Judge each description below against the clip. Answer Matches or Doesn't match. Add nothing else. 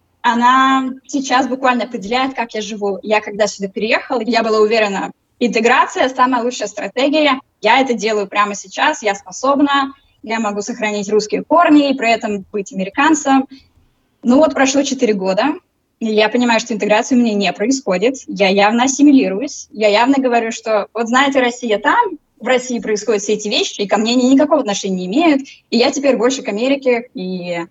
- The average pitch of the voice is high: Matches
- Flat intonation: Doesn't match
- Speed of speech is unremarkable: Doesn't match